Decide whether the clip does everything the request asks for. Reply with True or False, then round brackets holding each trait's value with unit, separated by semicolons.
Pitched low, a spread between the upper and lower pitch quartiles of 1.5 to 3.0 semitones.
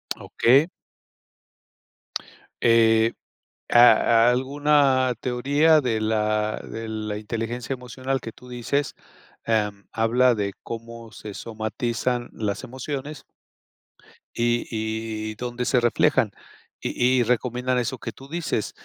True (120 Hz; 2.4 semitones)